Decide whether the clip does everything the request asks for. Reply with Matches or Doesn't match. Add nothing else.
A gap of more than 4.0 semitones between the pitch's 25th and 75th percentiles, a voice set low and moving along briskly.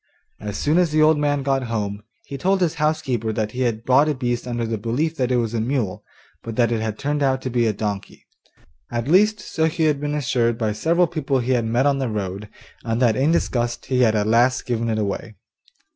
Matches